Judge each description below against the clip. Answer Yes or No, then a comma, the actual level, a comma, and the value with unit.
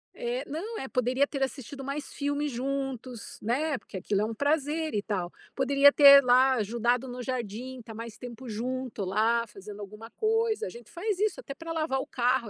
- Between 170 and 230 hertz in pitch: No, very high, 255 Hz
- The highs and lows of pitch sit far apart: No, average, 3.7 semitones